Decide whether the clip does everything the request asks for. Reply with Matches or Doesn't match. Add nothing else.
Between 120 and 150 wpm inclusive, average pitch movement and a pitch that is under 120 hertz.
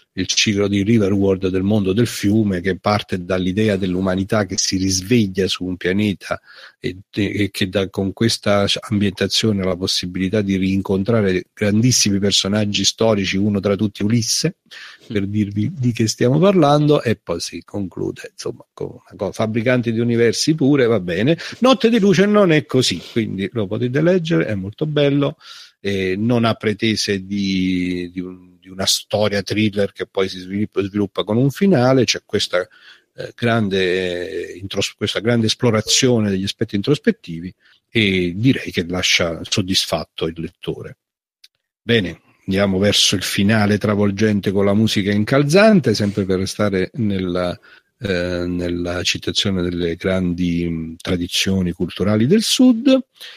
Matches